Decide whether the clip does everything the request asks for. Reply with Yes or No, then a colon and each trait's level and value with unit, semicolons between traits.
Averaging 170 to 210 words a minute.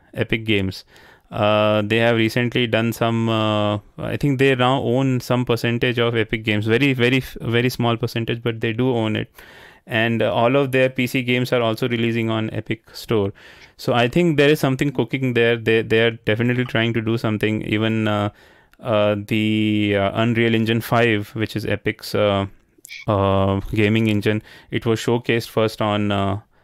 Yes: average, 180 wpm